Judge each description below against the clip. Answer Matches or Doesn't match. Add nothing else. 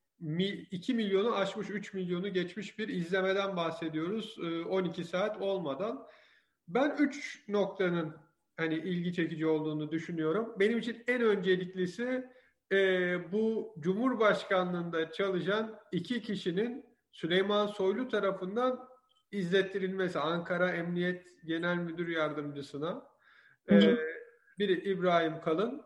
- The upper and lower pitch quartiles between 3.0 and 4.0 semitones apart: Matches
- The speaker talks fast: Doesn't match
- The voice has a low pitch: Doesn't match